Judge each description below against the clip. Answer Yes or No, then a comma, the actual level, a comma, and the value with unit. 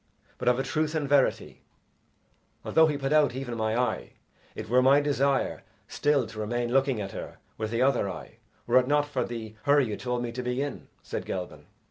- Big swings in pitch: No, average, 3.2 semitones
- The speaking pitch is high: No, low, 130 Hz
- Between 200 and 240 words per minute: Yes, fast, 205 wpm